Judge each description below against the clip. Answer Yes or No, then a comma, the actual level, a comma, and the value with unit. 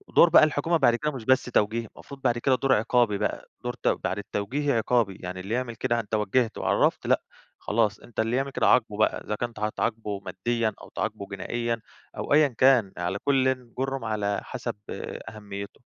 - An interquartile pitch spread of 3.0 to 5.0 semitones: Yes, average, 3.7 semitones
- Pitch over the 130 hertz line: No, low, 115 Hz